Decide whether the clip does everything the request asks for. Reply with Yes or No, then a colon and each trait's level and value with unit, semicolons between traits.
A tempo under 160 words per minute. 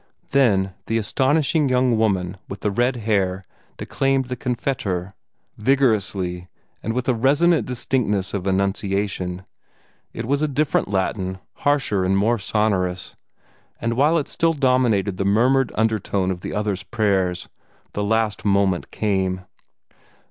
Yes: slow, 135 wpm